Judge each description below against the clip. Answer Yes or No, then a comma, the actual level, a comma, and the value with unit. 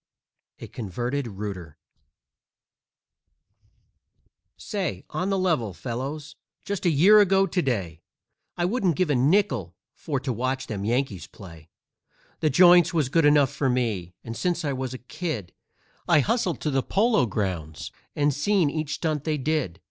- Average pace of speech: Yes, average, 155 wpm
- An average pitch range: No, wide, 7.2 semitones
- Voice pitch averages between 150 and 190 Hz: No, medium, 140 Hz